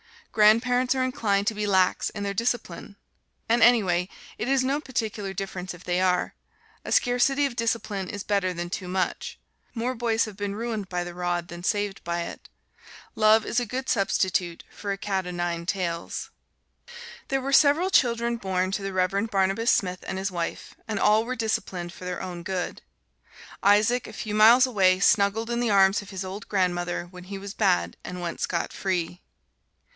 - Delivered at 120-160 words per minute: No, average, 185 wpm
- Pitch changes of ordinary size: Yes, average, 3.9 semitones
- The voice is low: No, high, 200 Hz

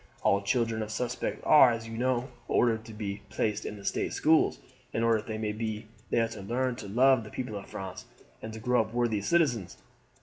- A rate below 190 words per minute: No, fast, 205 wpm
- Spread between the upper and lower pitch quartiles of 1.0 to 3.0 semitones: Yes, narrow, 2.6 semitones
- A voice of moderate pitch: No, low, 115 Hz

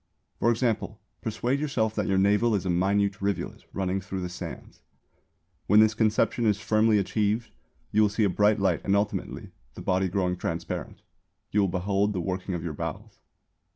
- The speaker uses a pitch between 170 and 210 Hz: No, low, 100 Hz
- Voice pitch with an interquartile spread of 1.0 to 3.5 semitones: Yes, narrow, 2.4 semitones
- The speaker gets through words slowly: No, average, 180 wpm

